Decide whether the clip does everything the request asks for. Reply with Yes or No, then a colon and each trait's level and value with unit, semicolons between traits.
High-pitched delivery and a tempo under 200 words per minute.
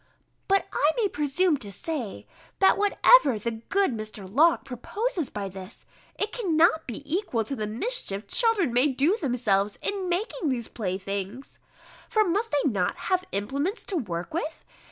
Yes: very high, 285 Hz; average, 160 wpm